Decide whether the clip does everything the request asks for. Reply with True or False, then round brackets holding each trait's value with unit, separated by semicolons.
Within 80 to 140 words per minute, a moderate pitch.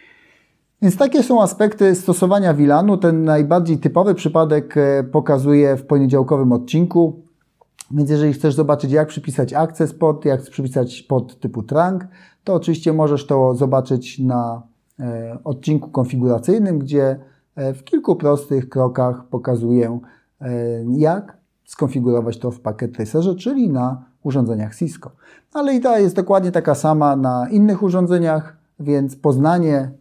True (125 wpm; 150 Hz)